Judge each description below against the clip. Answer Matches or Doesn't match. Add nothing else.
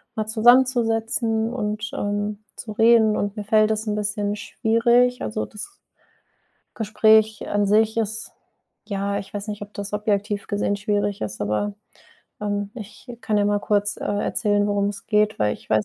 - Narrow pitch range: Matches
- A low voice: Doesn't match